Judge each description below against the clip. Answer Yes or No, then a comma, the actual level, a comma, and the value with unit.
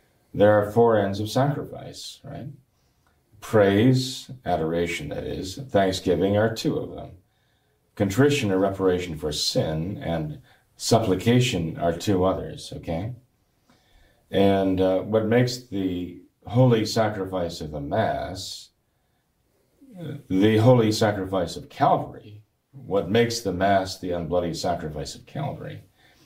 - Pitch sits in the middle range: No, low, 105 Hz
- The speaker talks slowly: Yes, slow, 120 wpm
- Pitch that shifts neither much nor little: Yes, average, 4.9 semitones